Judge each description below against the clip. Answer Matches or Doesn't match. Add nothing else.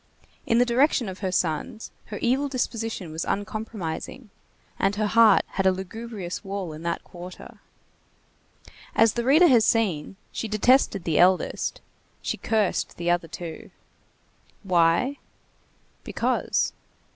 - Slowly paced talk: Matches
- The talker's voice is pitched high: Matches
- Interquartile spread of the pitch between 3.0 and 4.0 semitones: Doesn't match